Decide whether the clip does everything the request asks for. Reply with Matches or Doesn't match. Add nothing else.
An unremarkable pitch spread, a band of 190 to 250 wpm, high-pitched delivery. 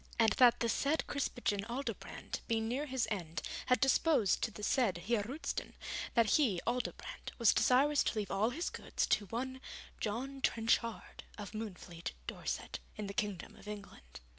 Doesn't match